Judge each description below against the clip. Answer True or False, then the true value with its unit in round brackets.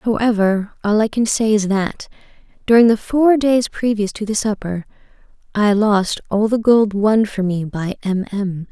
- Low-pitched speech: False (210 Hz)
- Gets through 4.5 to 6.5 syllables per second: False (4.3 syllables/s)